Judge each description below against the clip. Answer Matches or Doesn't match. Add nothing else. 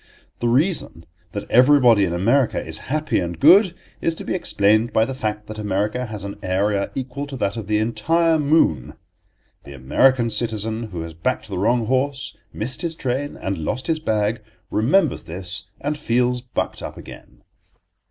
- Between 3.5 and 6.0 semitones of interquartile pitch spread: Matches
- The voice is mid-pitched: Doesn't match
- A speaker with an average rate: Matches